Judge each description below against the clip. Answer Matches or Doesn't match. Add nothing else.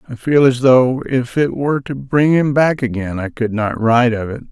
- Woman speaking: Doesn't match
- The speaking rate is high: Matches